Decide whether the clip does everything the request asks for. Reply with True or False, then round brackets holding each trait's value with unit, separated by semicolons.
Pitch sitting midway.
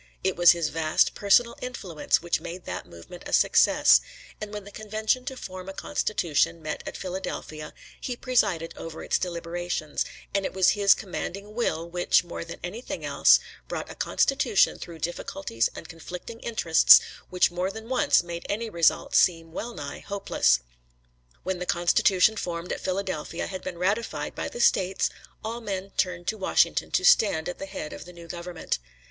True (180 Hz)